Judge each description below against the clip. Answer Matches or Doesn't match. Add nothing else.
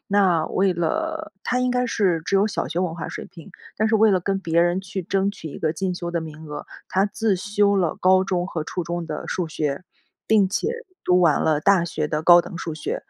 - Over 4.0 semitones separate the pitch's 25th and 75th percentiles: Doesn't match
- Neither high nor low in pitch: Matches